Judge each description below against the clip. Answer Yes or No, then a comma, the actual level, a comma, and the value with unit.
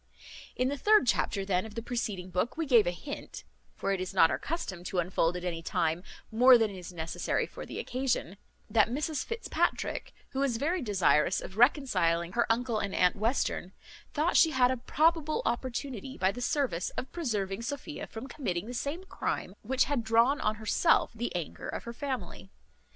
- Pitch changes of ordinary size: No, wide, 6.3 semitones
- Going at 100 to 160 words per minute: No, average, 190 wpm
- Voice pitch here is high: Yes, high, 235 Hz